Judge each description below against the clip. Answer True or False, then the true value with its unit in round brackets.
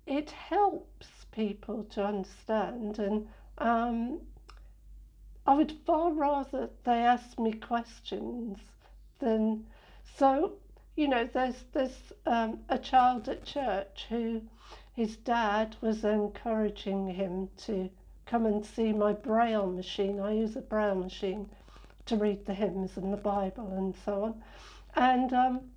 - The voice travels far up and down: False (3.7 semitones)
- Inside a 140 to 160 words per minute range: False (130 wpm)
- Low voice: False (225 Hz)